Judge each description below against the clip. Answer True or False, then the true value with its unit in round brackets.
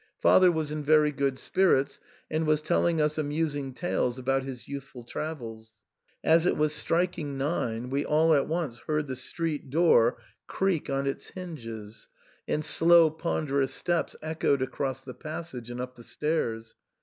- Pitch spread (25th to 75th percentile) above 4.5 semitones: False (3.5 semitones)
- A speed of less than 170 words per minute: True (160 wpm)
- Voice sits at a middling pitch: True (150 Hz)